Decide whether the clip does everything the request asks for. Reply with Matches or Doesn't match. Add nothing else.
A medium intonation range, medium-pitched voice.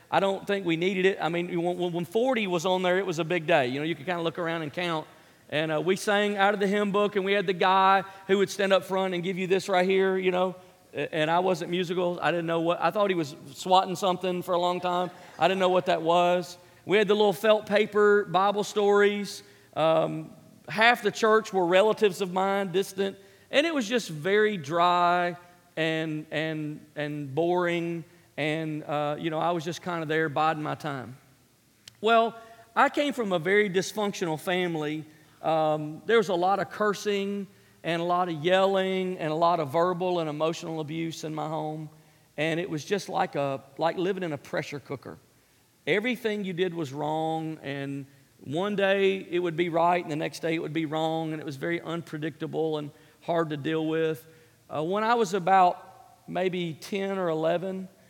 Matches